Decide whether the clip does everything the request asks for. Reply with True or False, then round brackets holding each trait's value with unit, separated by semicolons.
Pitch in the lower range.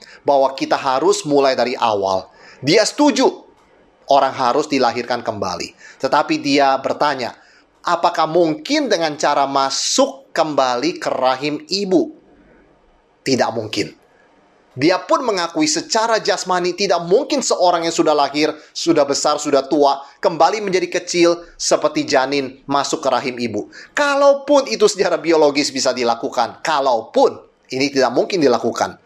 False (150 Hz)